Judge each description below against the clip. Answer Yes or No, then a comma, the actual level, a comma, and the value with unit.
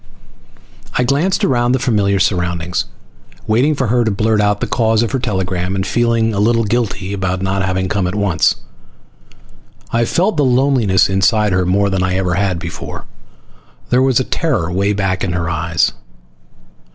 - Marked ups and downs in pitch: No, average, 4.2 semitones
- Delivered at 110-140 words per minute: No, average, 175 wpm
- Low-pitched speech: Yes, low, 100 Hz